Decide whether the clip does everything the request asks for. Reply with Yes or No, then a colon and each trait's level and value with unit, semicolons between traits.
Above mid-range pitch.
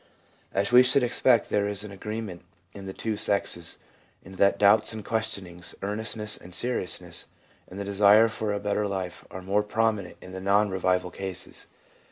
No: low, 100 Hz